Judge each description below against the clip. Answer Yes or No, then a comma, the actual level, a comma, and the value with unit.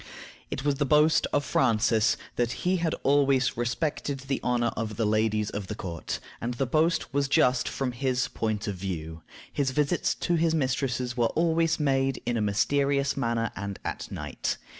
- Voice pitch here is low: Yes, low, 130 Hz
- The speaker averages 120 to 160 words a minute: No, average, 180 wpm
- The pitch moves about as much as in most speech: Yes, average, 4.0 semitones